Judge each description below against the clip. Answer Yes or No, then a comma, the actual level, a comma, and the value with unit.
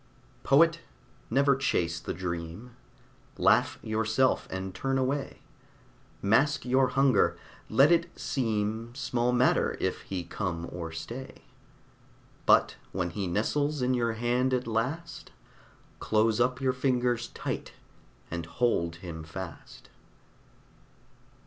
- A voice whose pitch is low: Yes, low, 120 Hz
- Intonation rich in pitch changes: Yes, wide, 5.7 semitones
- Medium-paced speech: No, slow, 115 wpm